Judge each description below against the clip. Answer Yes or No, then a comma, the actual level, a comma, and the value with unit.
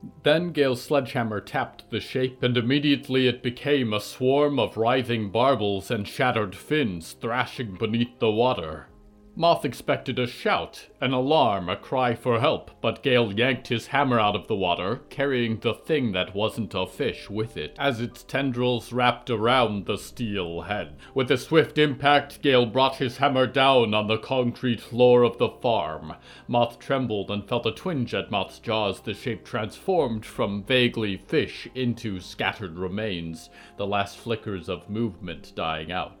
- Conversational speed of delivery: Yes, average, 165 wpm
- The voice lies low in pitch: Yes, low, 120 Hz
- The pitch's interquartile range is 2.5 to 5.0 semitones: Yes, average, 4.0 semitones